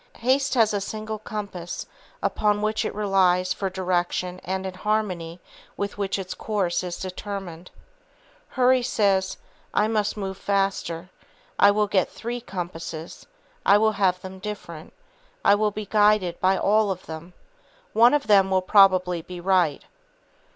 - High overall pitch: Yes, high, 195 Hz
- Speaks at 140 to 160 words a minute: Yes, average, 150 wpm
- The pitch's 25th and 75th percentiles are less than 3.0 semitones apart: Yes, narrow, 2.6 semitones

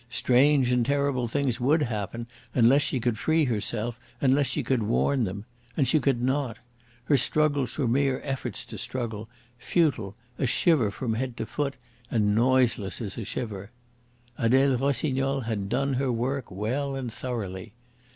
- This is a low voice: Yes, low, 125 Hz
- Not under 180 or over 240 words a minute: No, average, 160 wpm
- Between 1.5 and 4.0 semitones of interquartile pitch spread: Yes, average, 3.4 semitones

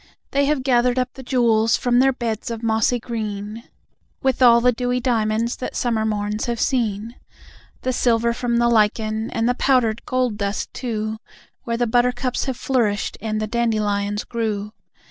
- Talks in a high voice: Yes, high, 235 Hz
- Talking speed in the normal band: Yes, average, 165 wpm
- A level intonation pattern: Yes, narrow, 2.3 semitones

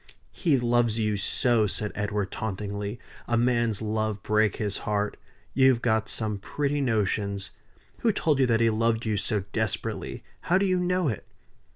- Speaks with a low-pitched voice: Yes, low, 110 Hz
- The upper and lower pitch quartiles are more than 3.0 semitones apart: No, average, 2.7 semitones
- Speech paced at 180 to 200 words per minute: No, average, 165 wpm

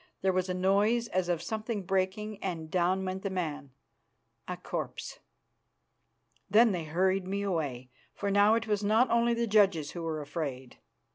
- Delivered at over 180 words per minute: No, average, 165 wpm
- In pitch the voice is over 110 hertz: Yes, high, 190 Hz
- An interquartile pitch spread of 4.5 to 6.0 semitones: No, average, 3.6 semitones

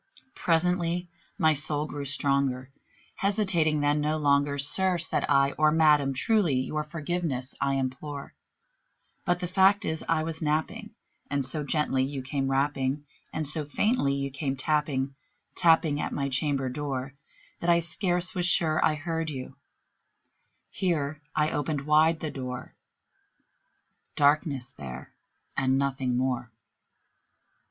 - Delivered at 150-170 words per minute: No, slow, 135 wpm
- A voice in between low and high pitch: Yes, medium, 150 Hz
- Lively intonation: No, average, 2.9 semitones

